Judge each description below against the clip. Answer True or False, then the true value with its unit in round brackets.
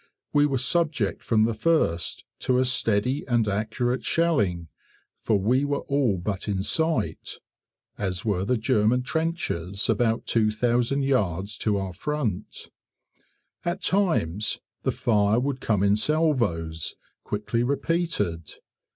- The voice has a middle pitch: False (115 Hz)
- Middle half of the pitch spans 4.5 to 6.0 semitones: True (5.5 semitones)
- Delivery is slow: True (125 wpm)